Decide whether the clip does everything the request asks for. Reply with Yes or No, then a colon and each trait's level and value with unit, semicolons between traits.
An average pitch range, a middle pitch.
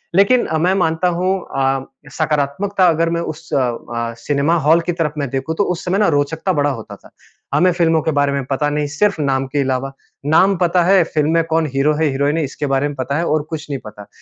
Yes: average, 3.4 semitones; medium, 150 Hz